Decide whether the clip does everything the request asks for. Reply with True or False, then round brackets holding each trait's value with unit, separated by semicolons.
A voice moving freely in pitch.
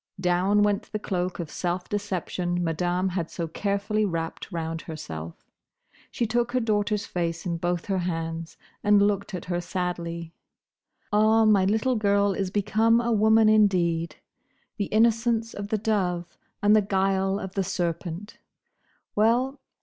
False (3.4 semitones)